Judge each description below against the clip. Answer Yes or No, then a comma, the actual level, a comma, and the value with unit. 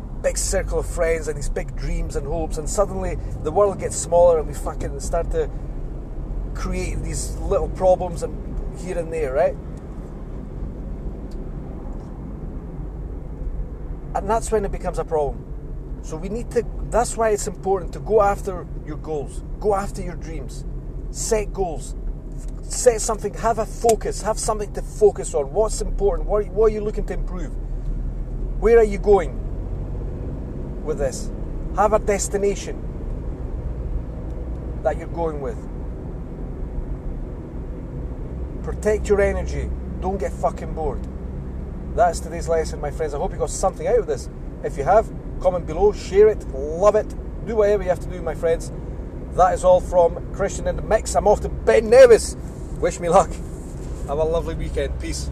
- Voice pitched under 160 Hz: No, medium, 165 Hz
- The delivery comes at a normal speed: Yes, average, 155 wpm